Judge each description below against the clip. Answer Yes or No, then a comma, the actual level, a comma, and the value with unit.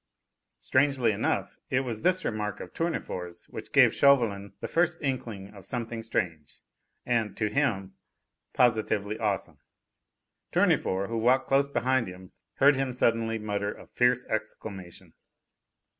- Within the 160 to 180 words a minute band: No, slow, 135 wpm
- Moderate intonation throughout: Yes, average, 4.4 semitones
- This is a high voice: No, low, 115 Hz